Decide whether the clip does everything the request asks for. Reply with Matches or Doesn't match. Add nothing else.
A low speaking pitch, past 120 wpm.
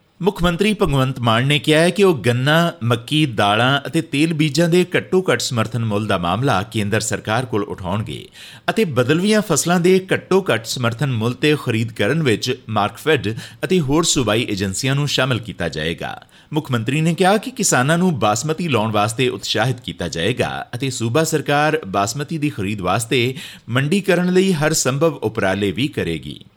Matches